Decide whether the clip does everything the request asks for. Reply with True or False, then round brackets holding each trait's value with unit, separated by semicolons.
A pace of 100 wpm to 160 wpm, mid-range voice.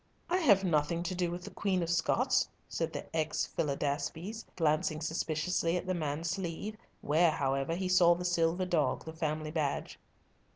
False (170 wpm; 170 Hz)